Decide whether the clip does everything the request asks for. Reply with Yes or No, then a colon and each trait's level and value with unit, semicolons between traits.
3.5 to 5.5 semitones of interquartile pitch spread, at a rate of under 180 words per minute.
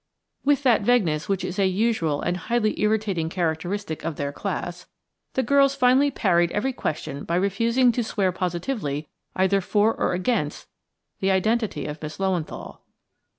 Yes: average, 5.2 semitones; average, 150 wpm